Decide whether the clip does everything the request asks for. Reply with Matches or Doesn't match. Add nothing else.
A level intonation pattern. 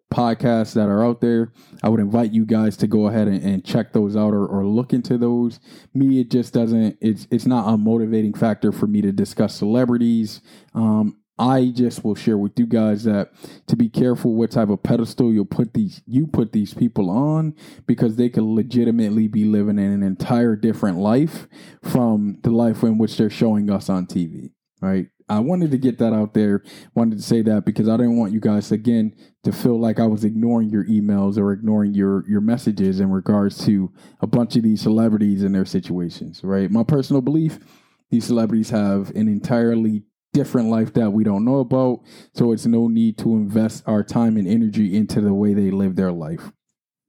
Matches